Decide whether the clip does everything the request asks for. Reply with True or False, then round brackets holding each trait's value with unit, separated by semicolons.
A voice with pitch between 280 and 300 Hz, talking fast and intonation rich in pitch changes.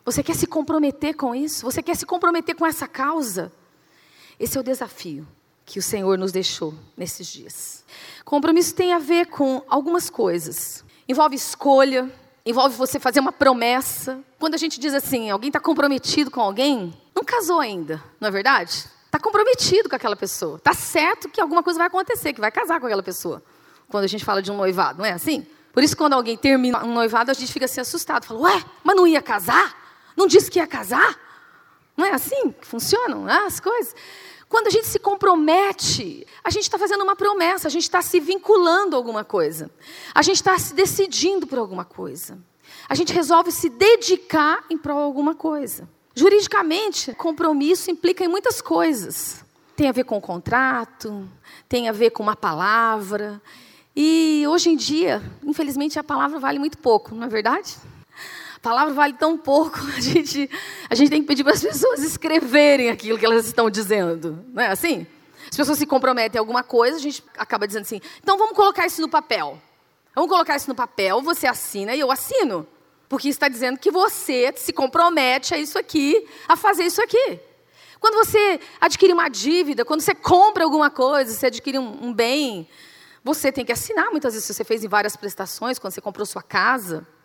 True (290 Hz; 190 wpm; 6.6 semitones)